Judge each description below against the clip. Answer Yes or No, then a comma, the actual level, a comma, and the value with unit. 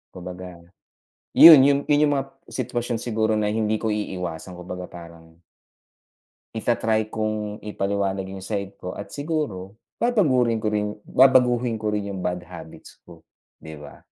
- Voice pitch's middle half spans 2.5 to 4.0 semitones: No, average, 4.6 semitones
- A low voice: Yes, low, 105 Hz